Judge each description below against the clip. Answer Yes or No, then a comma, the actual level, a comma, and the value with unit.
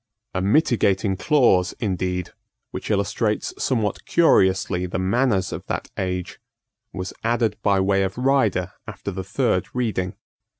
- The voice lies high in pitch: No, low, 100 Hz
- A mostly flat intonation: No, average, 3.9 semitones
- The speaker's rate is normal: No, slow, 130 wpm